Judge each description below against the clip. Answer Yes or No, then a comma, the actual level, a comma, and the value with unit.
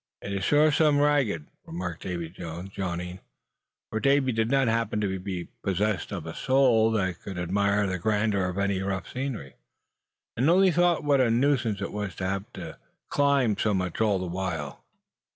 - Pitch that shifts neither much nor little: No, wide, 5.8 semitones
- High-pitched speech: No, low, 100 Hz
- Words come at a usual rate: Yes, average, 185 wpm